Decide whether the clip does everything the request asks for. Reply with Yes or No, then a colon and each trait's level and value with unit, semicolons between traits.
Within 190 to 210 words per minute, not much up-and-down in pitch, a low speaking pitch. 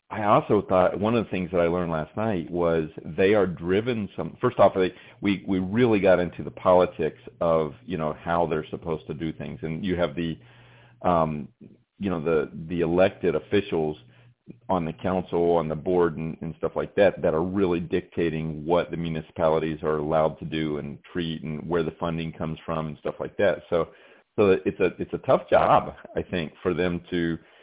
Yes: average, 200 wpm; narrow, 2.3 semitones; very low, 85 Hz